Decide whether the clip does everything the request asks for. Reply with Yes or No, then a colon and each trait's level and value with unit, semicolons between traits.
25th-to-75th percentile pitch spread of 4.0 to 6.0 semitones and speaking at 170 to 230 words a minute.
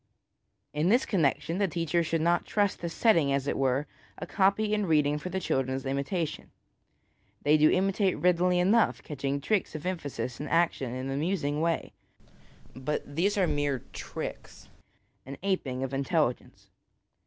No: average, 4.7 semitones; average, 155 wpm